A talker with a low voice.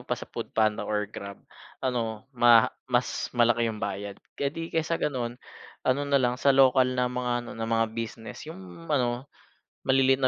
Yes: low, 120 Hz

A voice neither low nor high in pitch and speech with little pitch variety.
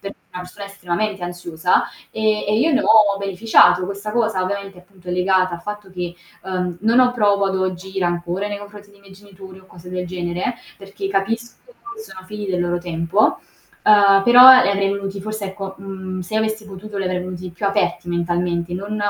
No: high, 195 Hz; narrow, 2.3 semitones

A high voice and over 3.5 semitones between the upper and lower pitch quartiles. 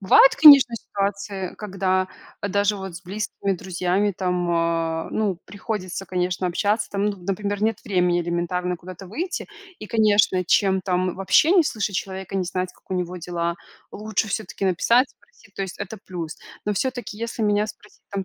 No: high, 195 Hz; narrow, 2.6 semitones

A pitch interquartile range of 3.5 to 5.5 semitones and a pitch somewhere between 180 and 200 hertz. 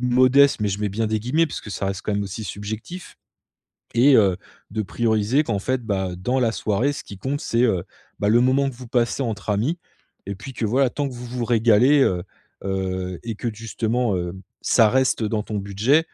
No: average, 3.9 semitones; low, 115 Hz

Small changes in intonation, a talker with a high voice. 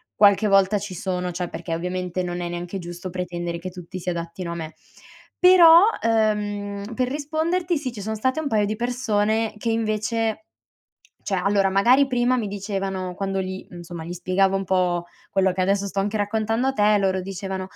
No: average, 3.4 semitones; high, 195 Hz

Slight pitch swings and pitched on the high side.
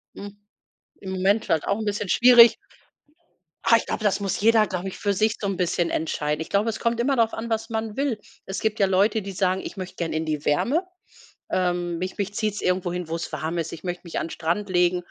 No: average, 3.7 semitones; high, 195 Hz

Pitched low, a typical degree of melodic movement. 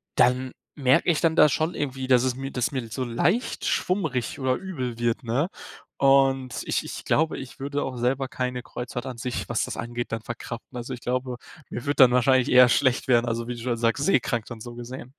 No: low, 125 Hz; narrow, 2.1 semitones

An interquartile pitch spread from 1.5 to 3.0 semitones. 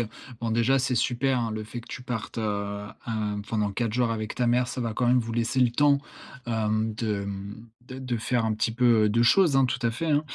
Yes: narrow, 2.5 semitones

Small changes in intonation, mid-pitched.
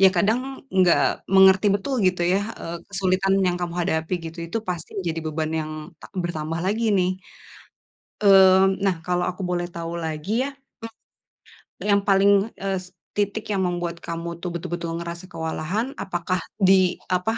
Yes: narrow, 2.3 semitones; medium, 180 Hz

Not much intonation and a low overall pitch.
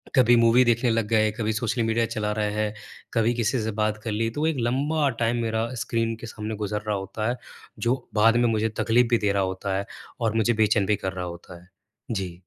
Yes: narrow, 1.9 semitones; low, 110 Hz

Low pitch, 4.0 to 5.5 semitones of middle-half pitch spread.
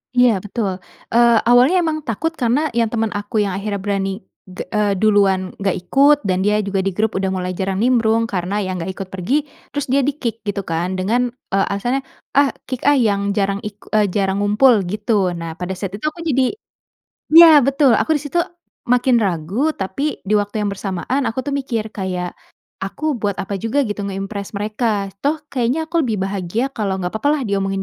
No: high, 210 Hz; average, 4.4 semitones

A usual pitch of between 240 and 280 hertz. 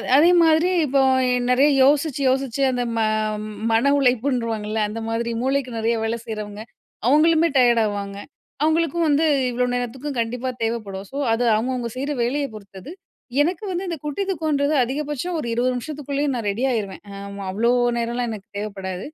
Yes: very high, 250 Hz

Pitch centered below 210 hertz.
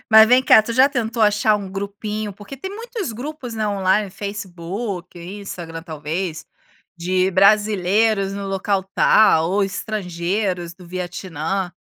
Yes: high, 200 Hz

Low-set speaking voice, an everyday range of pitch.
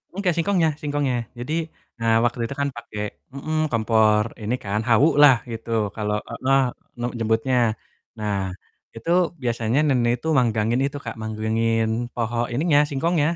Yes: low, 120 Hz; average, 4.1 semitones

